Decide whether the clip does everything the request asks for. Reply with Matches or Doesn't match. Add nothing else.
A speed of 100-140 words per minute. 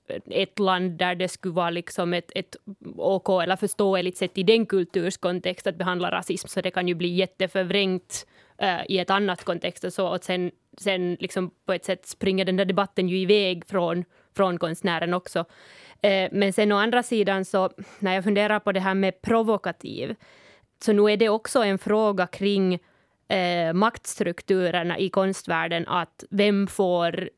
Doesn't match